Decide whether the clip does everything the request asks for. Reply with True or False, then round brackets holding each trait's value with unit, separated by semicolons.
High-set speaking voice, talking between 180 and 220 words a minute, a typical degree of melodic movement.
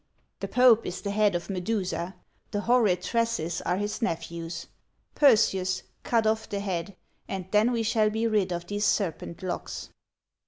False (205 Hz; 160 wpm; 3.6 semitones)